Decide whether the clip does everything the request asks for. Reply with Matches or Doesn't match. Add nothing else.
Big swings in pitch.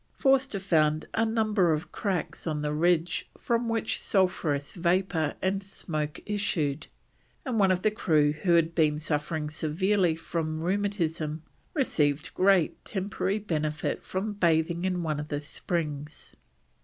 Doesn't match